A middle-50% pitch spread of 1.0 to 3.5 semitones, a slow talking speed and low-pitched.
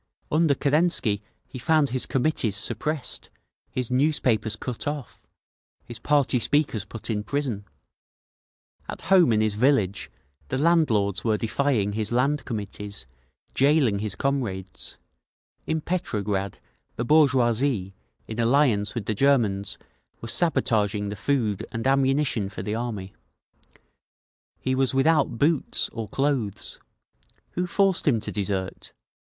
No: wide, 5.4 semitones; slow, 125 wpm; low, 120 Hz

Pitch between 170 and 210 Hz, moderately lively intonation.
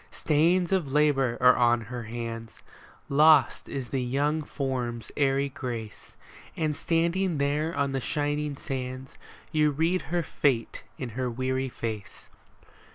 No: low, 135 Hz; average, 3.5 semitones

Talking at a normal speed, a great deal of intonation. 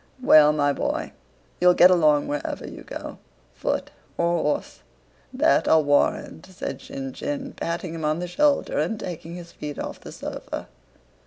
Yes: average, 145 wpm; wide, 6.7 semitones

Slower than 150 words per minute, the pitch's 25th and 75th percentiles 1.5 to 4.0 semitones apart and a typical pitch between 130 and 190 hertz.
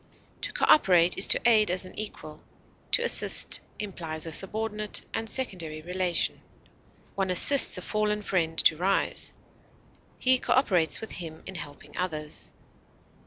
No: slow, 135 wpm; average, 4.4 semitones; medium, 185 Hz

